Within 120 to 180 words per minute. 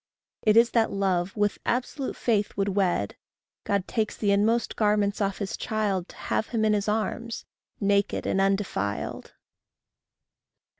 Yes: average, 145 wpm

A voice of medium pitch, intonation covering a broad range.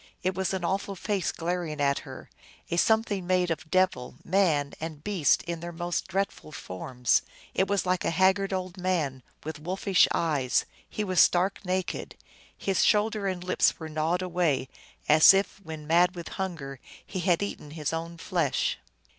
No: medium, 175 Hz; average, 3.2 semitones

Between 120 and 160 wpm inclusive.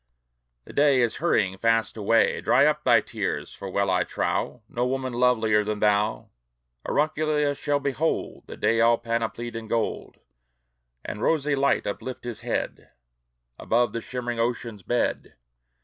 Yes: average, 150 wpm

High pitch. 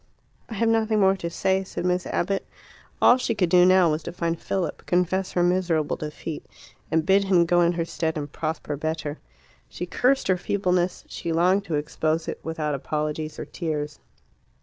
No: medium, 175 Hz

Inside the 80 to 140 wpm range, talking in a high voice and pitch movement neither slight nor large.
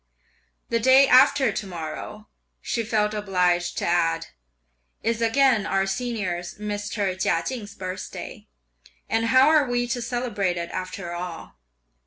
Yes: slow, 135 wpm; high, 210 Hz; average, 5.0 semitones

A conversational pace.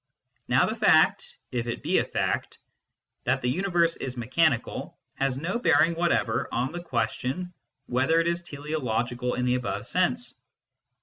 Yes: average, 160 wpm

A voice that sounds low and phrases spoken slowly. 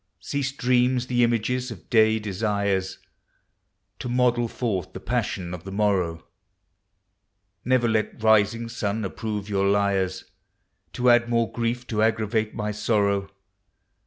Yes: low, 110 Hz; slow, 130 wpm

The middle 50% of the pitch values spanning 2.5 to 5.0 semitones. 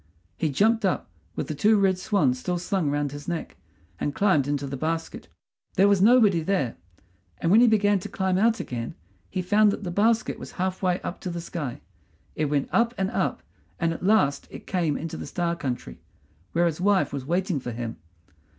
No: wide, 5.5 semitones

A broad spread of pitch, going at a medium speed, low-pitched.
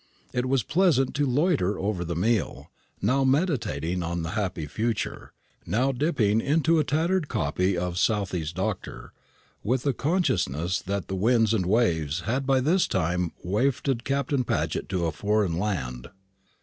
Yes: wide, 7.2 semitones; average, 150 wpm; low, 110 Hz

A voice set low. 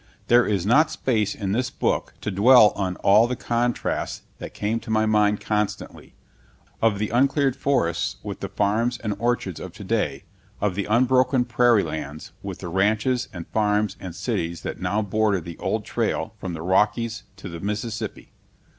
Yes: low, 105 Hz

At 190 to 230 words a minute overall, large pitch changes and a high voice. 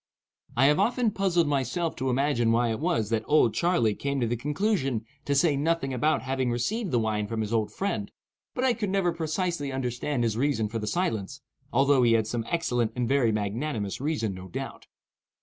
No: average, 200 wpm; wide, 6.0 semitones; low, 135 Hz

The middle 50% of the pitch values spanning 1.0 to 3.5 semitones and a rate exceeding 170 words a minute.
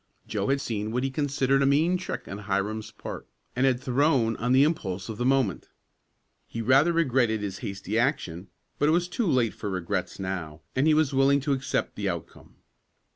No: average, 5.2 semitones; average, 195 wpm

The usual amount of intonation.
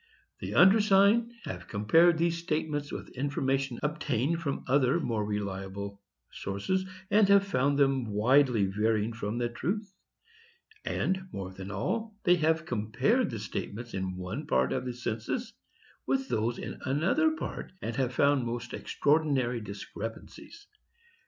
No: wide, 7.7 semitones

